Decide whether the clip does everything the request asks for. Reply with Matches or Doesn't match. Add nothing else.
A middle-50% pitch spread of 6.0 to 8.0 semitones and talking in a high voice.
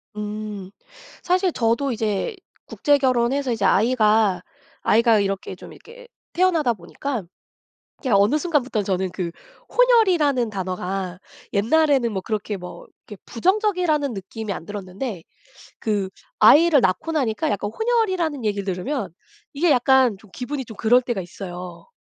Matches